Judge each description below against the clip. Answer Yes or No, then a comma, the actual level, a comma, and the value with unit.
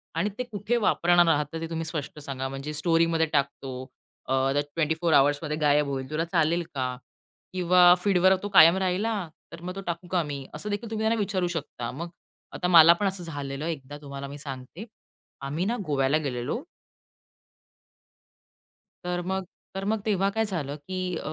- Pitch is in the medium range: Yes, medium, 165 Hz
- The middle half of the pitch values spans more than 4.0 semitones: Yes, average, 4.4 semitones